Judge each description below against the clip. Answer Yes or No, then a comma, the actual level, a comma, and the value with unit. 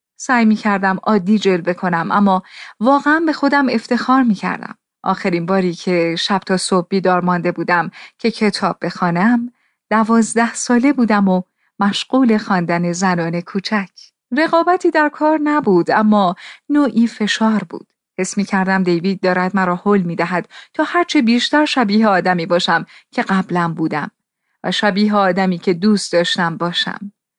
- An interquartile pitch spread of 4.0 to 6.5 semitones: Yes, average, 4.5 semitones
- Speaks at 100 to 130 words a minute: No, average, 145 wpm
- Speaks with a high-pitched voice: Yes, high, 200 Hz